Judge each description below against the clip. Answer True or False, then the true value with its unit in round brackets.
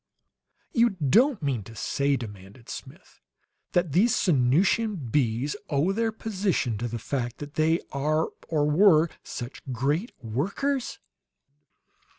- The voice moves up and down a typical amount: False (7.7 semitones)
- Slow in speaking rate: True (125 wpm)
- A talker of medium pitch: True (150 Hz)